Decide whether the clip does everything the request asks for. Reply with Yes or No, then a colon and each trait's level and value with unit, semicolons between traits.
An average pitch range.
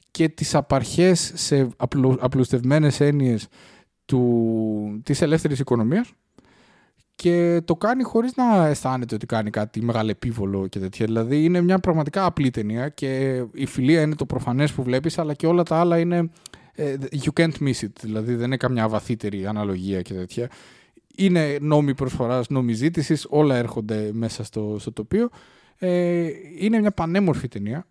No: wide, 6.2 semitones